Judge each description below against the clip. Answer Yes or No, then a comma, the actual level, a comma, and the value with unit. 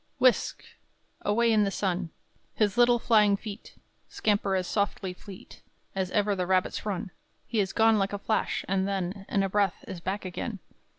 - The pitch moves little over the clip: Yes, narrow, 1.9 semitones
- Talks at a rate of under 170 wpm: No, average, 175 wpm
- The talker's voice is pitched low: No, high, 200 Hz